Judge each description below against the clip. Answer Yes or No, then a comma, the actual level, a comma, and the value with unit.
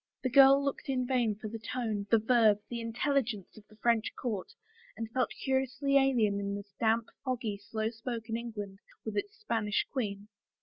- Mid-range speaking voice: No, high, 230 Hz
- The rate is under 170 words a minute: No, average, 175 wpm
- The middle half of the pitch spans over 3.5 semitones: No, average, 3.2 semitones